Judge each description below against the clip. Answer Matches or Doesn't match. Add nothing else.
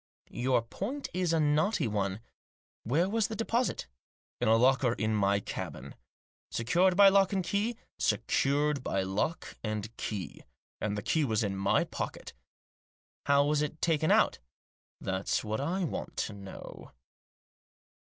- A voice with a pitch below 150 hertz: Matches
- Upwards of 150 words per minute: Matches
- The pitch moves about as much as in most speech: Doesn't match